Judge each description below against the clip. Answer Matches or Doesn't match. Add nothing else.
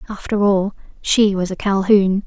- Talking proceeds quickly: Doesn't match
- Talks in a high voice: Matches